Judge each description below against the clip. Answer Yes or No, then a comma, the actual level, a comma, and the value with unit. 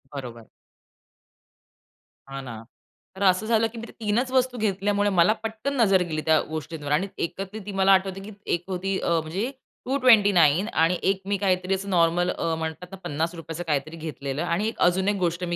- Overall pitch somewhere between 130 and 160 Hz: No, medium, 185 Hz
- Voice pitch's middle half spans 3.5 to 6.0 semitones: Yes, average, 4.1 semitones